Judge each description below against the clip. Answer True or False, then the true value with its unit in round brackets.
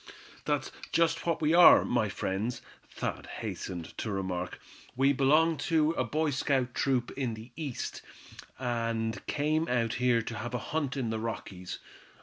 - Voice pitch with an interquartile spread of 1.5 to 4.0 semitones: False (5.1 semitones)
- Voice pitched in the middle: False (125 Hz)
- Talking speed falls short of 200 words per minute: True (155 wpm)